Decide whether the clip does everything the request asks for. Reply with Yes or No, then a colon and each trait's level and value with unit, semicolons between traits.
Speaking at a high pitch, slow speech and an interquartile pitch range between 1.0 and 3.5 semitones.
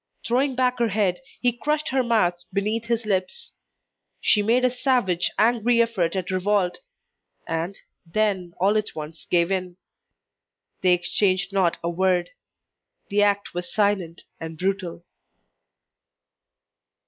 No: high, 195 Hz; slow, 130 wpm; average, 4.5 semitones